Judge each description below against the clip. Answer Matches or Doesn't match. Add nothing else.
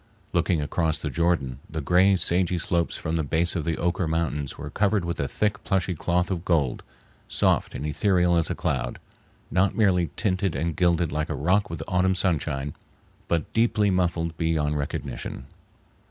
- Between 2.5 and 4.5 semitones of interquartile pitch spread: Matches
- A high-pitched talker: Doesn't match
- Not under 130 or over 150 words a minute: Doesn't match